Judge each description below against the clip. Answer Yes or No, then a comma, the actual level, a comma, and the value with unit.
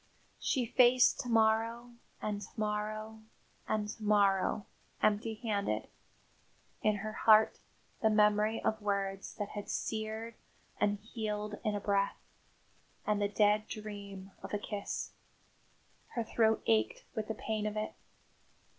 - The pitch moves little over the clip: Yes, narrow, 1.2 semitones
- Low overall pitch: No, high, 215 Hz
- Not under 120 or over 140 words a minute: Yes, slow, 135 wpm